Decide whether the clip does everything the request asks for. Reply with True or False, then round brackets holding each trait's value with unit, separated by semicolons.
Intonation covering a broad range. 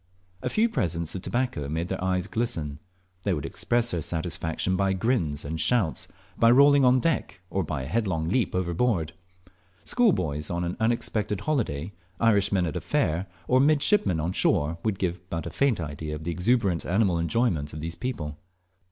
True (6.4 semitones)